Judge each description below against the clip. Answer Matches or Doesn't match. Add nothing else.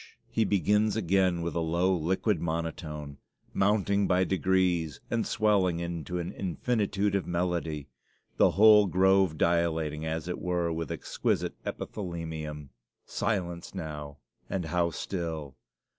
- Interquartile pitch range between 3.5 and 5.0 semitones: Doesn't match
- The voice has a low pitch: Matches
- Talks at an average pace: Doesn't match